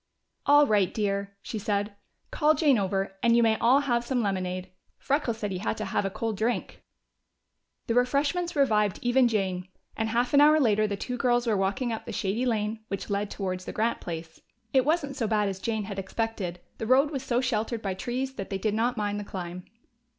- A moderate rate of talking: No, fast, 210 wpm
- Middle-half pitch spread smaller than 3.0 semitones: No, average, 3.9 semitones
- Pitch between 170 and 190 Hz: No, high, 220 Hz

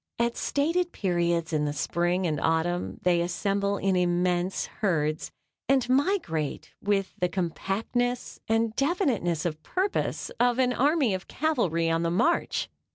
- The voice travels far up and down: Yes, wide, 6.4 semitones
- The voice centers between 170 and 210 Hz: Yes, high, 190 Hz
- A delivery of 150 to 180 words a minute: No, average, 140 wpm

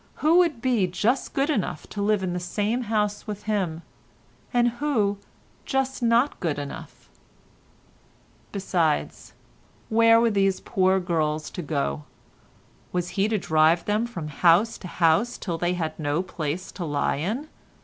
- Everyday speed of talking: Yes, average, 150 wpm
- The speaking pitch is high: Yes, high, 195 Hz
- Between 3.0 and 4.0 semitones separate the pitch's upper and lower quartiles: No, wide, 5.4 semitones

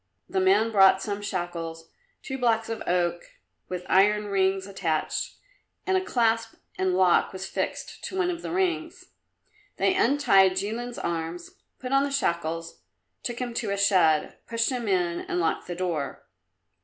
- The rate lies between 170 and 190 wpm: No, average, 160 wpm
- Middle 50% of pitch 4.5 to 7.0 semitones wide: Yes, average, 5.1 semitones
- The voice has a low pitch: No, high, 195 Hz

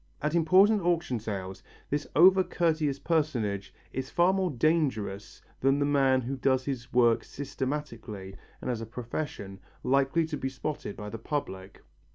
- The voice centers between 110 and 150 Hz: Yes, low, 135 Hz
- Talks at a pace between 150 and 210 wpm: Yes, average, 155 wpm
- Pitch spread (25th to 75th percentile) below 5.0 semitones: No, wide, 5.4 semitones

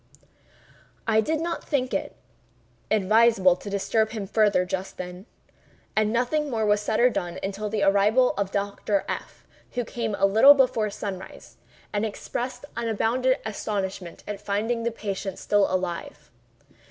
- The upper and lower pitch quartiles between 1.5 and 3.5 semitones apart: Yes, average, 2.9 semitones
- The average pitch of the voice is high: Yes, high, 210 Hz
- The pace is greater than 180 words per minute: No, average, 145 wpm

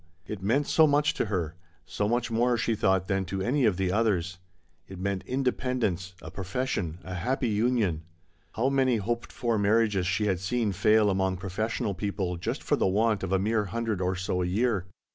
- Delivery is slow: No, average, 200 wpm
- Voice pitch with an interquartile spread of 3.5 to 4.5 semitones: Yes, average, 3.8 semitones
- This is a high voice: No, low, 105 Hz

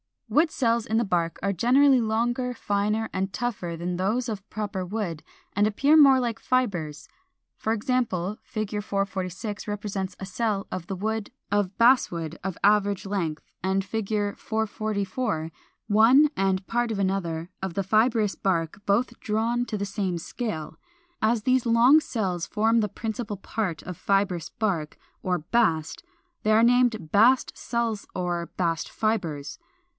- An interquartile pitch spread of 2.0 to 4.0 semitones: Yes, average, 3.6 semitones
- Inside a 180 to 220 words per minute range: No, average, 155 wpm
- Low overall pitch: No, high, 205 Hz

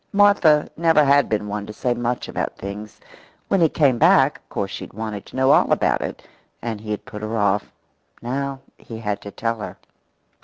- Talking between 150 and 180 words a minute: No, fast, 205 wpm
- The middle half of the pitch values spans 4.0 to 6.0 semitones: Yes, average, 5.2 semitones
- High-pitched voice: No, low, 115 Hz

